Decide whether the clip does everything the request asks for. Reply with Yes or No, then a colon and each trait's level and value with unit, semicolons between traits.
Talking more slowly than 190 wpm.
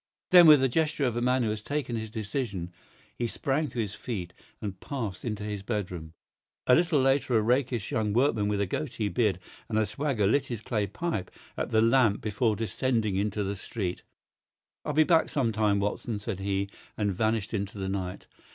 No: average, 195 wpm